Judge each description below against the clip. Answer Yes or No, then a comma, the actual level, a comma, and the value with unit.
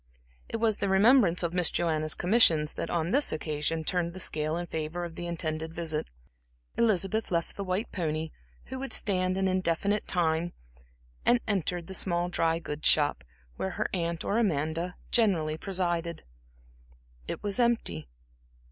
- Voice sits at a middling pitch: Yes, medium, 175 Hz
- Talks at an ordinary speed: Yes, average, 155 wpm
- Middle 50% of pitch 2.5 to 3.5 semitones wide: Yes, average, 3.2 semitones